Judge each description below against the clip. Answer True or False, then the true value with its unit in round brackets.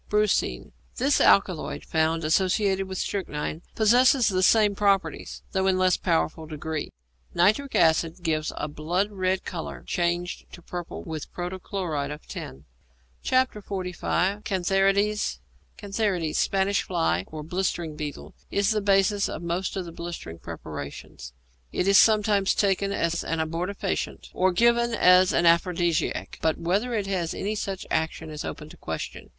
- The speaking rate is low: False (145 wpm)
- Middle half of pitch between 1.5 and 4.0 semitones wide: True (3.5 semitones)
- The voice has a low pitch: False (185 Hz)